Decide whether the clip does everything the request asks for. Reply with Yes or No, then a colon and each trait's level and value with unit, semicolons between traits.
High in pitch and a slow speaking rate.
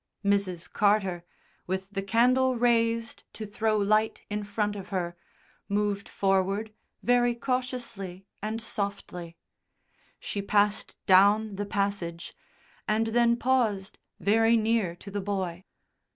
Yes: high, 205 Hz; slow, 120 wpm